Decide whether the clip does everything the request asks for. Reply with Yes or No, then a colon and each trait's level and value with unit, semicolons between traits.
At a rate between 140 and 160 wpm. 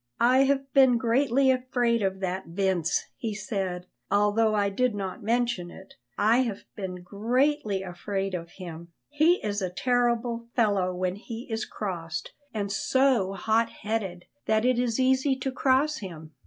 Yes: average, 155 wpm